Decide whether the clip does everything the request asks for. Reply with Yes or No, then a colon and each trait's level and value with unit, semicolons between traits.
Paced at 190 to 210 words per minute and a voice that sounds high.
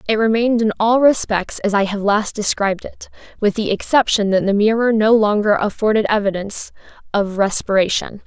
No: average, 165 wpm; high, 210 Hz